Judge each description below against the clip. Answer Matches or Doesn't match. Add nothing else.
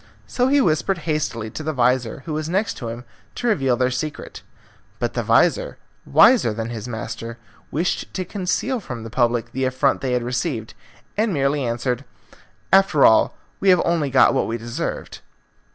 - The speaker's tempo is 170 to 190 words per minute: Matches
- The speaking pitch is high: Doesn't match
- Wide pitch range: Matches